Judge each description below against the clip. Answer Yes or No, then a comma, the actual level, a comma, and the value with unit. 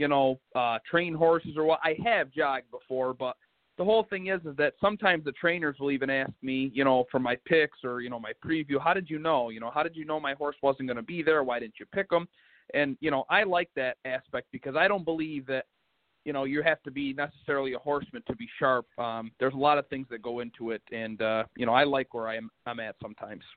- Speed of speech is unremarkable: No, fast, 260 wpm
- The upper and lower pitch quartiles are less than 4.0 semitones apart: No, average, 4.3 semitones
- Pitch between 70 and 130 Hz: No, medium, 140 Hz